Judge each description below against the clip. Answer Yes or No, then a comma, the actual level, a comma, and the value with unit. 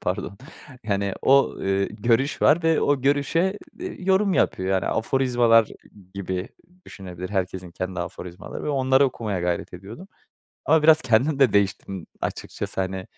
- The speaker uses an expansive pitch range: Yes, wide, 6.8 semitones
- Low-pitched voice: Yes, low, 110 Hz